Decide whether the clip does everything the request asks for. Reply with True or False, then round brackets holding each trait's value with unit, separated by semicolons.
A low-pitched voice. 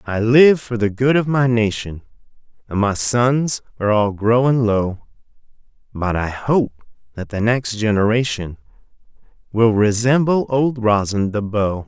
True (115 Hz)